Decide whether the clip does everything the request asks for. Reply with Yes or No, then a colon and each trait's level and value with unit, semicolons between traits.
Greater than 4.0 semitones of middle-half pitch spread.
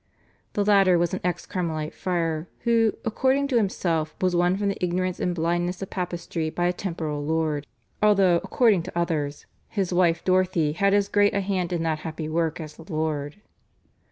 No: average, 3.2 semitones